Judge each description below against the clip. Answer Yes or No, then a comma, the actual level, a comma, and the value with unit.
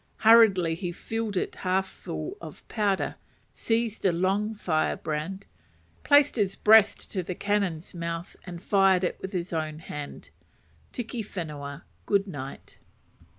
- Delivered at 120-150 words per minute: Yes, slow, 135 wpm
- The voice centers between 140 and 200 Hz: Yes, high, 190 Hz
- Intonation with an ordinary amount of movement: Yes, average, 3.8 semitones